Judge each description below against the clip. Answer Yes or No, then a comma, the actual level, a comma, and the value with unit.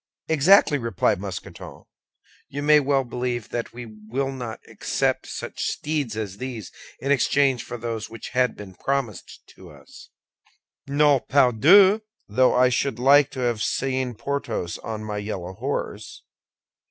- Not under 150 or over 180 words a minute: No, average, 140 wpm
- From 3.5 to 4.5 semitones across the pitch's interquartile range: Yes, average, 4.1 semitones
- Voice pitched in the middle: No, low, 125 Hz